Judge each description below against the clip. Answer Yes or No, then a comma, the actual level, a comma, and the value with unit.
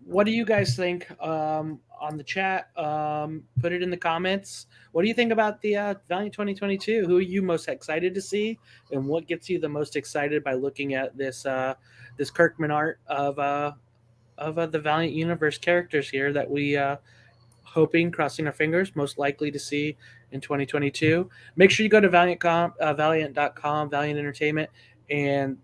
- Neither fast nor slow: Yes, average, 185 wpm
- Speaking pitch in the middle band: Yes, medium, 150 Hz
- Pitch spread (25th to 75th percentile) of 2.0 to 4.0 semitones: Yes, average, 3.7 semitones